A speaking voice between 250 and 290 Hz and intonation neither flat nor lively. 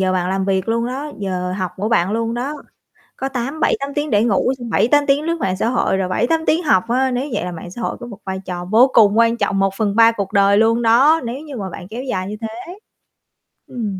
No: high, 225 Hz; average, 5.0 semitones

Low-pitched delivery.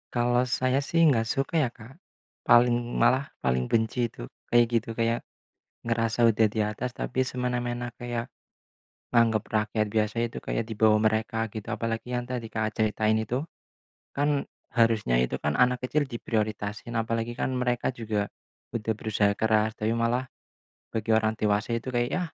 Yes: low, 115 Hz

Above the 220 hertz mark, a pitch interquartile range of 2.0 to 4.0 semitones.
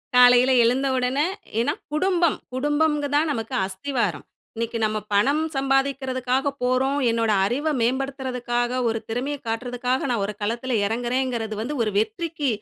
Yes: very high, 255 Hz; average, 2.9 semitones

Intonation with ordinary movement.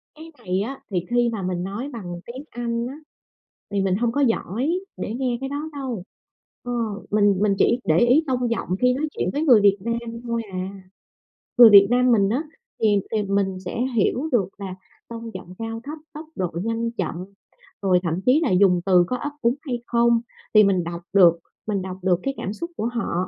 Yes: average, 4.4 semitones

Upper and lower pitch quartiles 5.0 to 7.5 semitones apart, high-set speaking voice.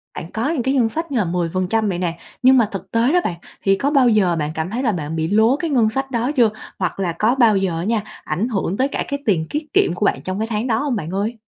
Yes: wide, 5.6 semitones; high, 215 Hz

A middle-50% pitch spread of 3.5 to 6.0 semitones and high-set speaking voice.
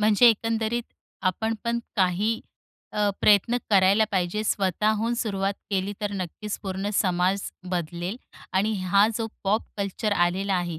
No: narrow, 2.6 semitones; high, 200 Hz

